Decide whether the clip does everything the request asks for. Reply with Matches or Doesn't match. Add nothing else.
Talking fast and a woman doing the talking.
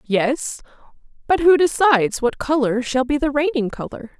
Doesn't match